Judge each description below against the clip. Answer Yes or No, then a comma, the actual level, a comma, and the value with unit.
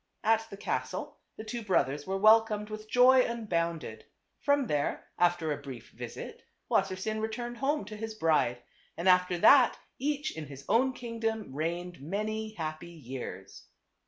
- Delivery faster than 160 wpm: No, average, 150 wpm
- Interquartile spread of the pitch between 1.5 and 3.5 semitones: No, wide, 5.6 semitones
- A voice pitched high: Yes, high, 210 Hz